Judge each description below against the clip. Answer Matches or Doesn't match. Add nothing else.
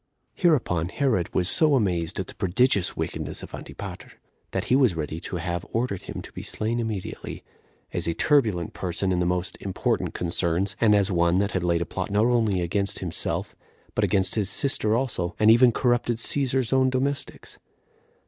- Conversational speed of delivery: Matches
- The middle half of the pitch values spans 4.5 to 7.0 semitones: Matches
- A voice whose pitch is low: Matches